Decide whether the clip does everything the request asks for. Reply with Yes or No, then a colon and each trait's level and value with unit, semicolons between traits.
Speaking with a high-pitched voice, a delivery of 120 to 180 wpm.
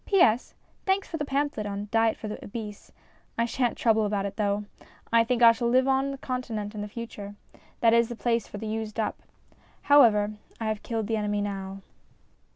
No: high, 225 Hz; average, 195 wpm